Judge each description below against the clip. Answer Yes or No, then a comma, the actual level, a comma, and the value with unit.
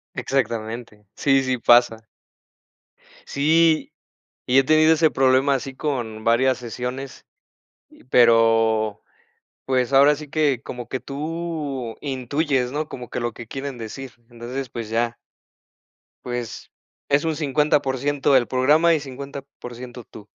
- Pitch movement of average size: Yes, average, 3.1 semitones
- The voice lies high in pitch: No, low, 130 Hz